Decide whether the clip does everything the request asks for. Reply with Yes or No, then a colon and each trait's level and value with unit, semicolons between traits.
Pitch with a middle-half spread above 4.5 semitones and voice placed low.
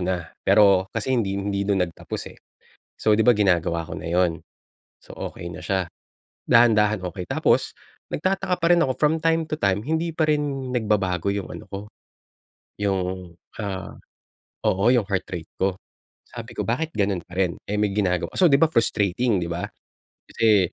Yes: average, 4.9 semitones; low, 100 Hz